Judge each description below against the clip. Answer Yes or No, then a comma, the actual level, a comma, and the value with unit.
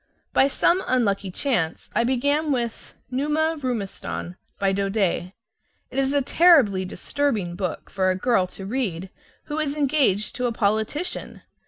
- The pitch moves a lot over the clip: Yes, wide, 6.6 semitones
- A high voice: Yes, high, 235 Hz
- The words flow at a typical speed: Yes, average, 145 wpm